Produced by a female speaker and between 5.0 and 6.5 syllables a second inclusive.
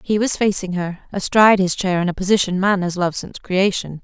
Yes: female; 6.0 syllables/s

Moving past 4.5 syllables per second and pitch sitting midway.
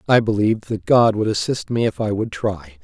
No: 5.3 syllables/s; low, 105 Hz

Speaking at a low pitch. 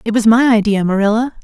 No: high, 220 Hz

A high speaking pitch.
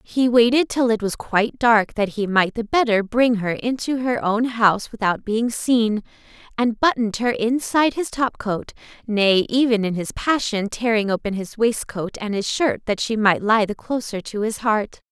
Yes: high, 225 Hz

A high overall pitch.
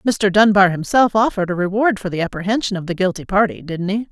Yes: high, 195 Hz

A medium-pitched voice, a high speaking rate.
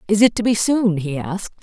No: high, 200 Hz; fast, 260 wpm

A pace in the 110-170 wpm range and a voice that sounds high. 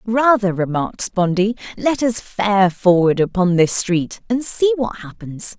Yes: average, 150 wpm; high, 205 Hz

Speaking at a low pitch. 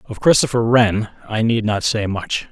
Yes: low, 110 Hz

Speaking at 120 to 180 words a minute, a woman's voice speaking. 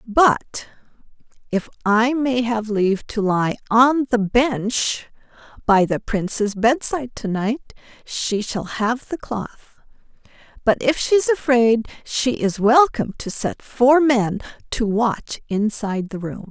Yes: average, 140 wpm; female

